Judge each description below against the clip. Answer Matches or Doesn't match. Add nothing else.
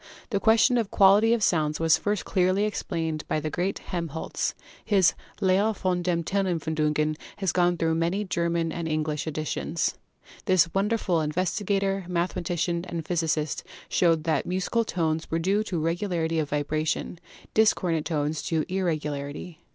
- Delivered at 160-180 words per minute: Doesn't match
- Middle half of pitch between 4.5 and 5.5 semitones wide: Doesn't match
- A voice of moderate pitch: Matches